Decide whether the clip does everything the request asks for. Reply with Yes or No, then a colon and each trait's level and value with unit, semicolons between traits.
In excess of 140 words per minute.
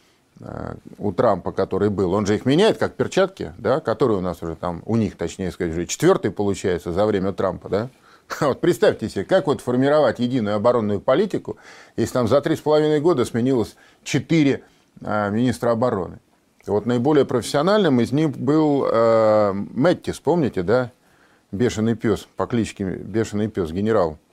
Yes: fast, 160 wpm